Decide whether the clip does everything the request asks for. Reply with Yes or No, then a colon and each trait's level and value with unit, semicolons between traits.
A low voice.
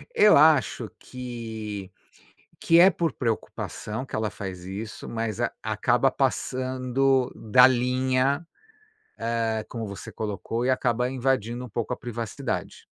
Yes: low, 120 Hz